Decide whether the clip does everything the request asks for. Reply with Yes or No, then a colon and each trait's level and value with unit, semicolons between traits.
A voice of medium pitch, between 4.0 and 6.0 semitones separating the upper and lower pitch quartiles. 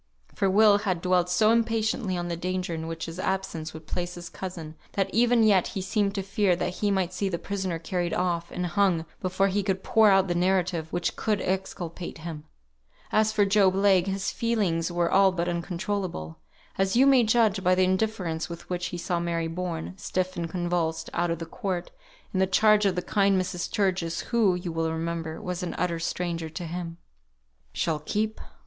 No: medium, 180 Hz; narrow, 2.6 semitones